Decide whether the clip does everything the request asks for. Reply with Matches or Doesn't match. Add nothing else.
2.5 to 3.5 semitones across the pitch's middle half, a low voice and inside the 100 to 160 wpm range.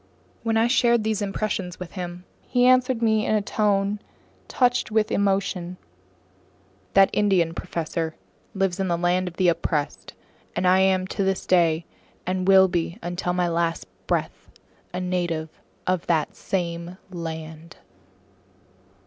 Doesn't match